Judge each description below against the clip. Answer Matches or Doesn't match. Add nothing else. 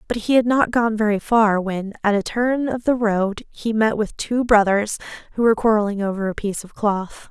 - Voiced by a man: Doesn't match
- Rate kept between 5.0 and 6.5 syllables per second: Matches